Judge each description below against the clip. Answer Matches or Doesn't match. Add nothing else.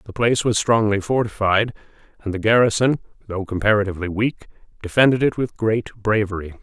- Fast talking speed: Doesn't match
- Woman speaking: Doesn't match